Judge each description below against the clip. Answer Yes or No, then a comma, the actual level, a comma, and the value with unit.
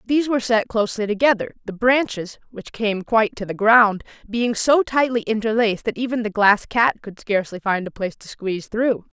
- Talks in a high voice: Yes, high, 220 Hz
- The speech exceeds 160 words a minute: Yes, average, 195 wpm